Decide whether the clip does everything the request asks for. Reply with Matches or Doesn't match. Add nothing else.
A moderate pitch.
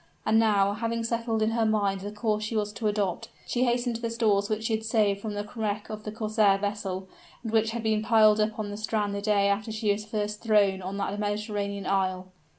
Doesn't match